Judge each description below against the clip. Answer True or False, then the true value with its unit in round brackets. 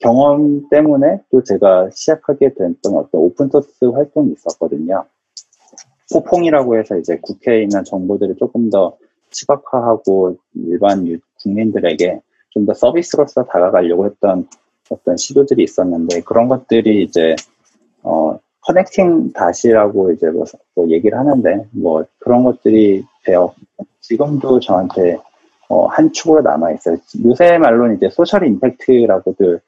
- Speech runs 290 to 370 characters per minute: True (300 characters per minute)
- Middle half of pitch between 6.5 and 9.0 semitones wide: True (7.7 semitones)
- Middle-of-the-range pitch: False (120 Hz)